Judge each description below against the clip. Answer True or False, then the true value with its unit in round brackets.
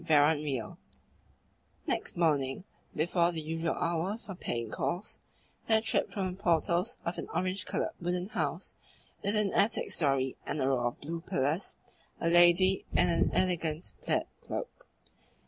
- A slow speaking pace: False (150 wpm)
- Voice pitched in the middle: True (170 Hz)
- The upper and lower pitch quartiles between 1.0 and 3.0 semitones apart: False (3.5 semitones)